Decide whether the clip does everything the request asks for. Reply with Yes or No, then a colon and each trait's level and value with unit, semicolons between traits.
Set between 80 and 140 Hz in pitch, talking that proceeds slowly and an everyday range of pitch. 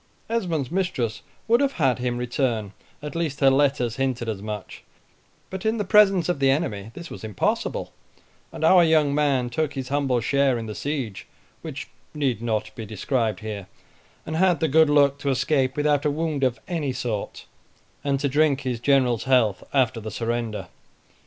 No: low, 135 Hz; average, 180 wpm; average, 4.4 semitones